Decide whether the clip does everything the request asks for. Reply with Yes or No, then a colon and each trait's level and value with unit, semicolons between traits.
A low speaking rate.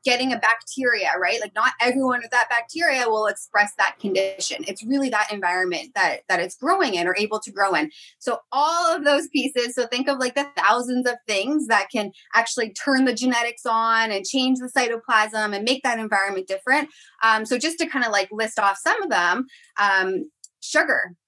No: average, 200 wpm